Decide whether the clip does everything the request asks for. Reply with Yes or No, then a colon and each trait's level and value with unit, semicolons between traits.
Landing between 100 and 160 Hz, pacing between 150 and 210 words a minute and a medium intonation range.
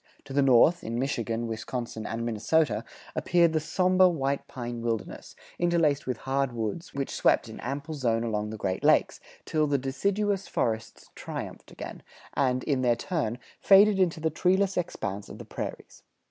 No: low, 135 Hz; average, 165 wpm; wide, 6.3 semitones